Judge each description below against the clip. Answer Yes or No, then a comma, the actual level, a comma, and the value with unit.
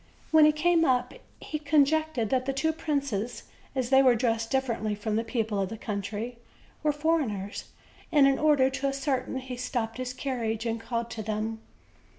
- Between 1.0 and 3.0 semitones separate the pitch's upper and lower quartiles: No, average, 4.0 semitones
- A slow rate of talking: No, average, 185 wpm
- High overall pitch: Yes, very high, 255 Hz